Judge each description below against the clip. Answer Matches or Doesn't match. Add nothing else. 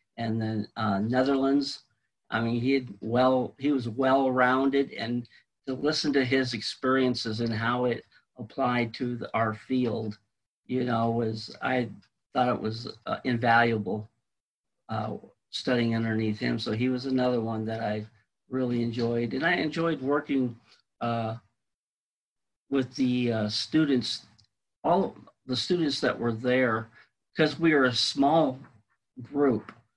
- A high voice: Doesn't match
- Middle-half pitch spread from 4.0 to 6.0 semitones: Doesn't match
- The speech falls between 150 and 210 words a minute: Doesn't match